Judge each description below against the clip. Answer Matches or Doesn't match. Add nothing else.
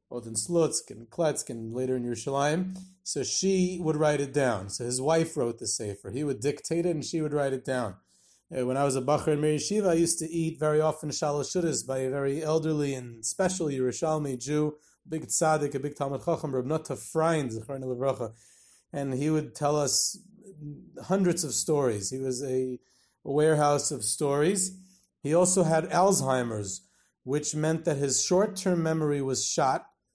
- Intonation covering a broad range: Doesn't match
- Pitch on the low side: Doesn't match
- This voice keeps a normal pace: Matches